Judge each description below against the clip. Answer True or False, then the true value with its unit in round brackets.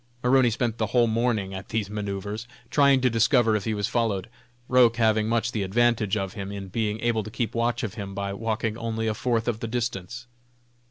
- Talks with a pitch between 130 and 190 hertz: False (110 Hz)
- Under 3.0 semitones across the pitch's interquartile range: True (2.4 semitones)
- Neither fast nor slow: False (210 wpm)